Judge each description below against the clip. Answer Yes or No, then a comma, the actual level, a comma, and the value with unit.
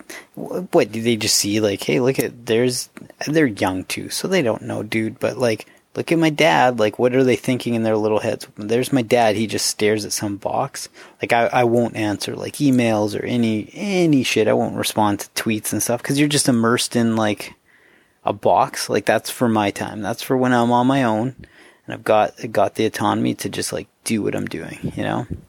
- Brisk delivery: Yes, fast, 225 wpm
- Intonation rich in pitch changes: No, average, 2.9 semitones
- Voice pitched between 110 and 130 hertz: Yes, low, 115 Hz